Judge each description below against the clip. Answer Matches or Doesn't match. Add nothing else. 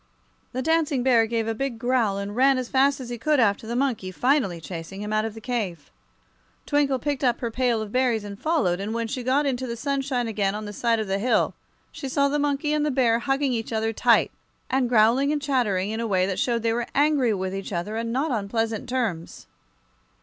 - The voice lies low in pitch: Doesn't match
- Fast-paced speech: Matches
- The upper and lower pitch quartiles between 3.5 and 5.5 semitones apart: Matches